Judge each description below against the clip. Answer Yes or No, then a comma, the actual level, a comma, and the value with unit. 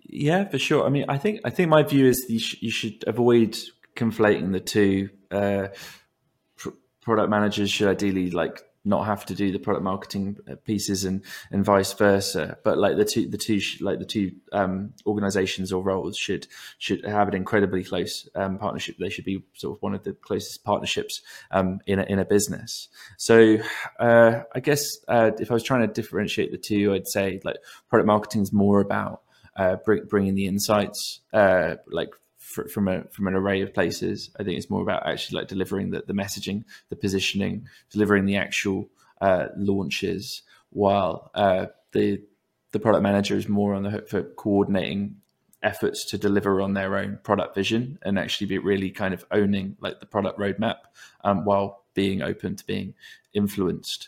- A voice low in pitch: Yes, low, 100 Hz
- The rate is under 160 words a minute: No, average, 190 wpm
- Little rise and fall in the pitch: Yes, narrow, 1.5 semitones